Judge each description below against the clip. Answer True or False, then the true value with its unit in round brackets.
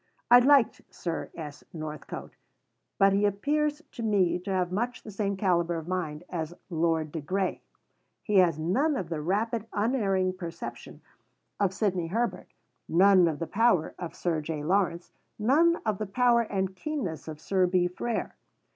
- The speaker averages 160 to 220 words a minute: True (165 wpm)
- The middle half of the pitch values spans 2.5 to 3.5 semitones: False (4.4 semitones)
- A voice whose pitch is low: False (190 Hz)